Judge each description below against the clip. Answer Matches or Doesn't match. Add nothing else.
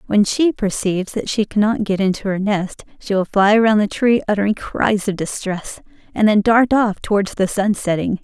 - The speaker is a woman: Matches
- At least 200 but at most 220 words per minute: Matches